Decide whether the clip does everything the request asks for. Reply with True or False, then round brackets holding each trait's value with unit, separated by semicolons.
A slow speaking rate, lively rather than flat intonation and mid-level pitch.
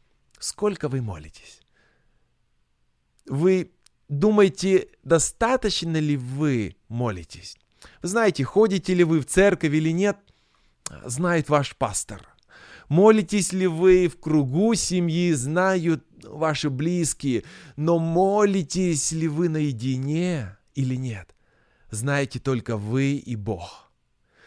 True (105 wpm; 5.7 semitones; 155 Hz)